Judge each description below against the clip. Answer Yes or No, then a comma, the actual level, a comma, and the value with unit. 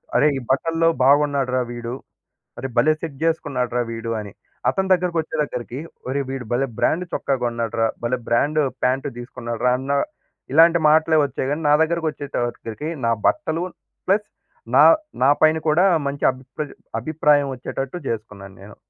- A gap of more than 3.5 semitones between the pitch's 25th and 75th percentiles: Yes, average, 4.6 semitones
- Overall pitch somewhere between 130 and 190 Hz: Yes, low, 135 Hz